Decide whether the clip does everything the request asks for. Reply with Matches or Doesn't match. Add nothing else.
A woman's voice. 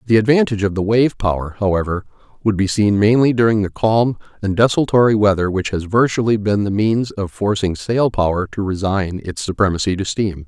Doesn't match